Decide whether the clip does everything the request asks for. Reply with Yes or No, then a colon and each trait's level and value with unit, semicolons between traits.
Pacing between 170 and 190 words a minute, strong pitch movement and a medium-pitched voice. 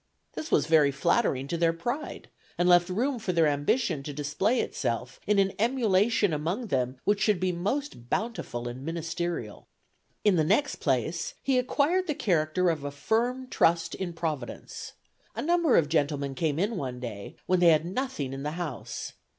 Yes: average, 175 wpm; wide, 7.2 semitones; medium, 170 Hz